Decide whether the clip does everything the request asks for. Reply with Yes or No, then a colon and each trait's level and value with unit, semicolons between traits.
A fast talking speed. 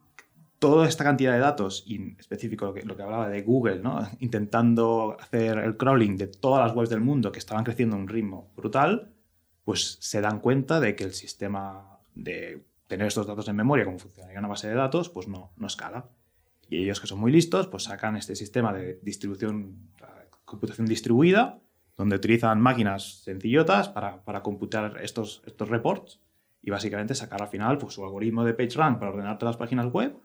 Yes: fast, 195 wpm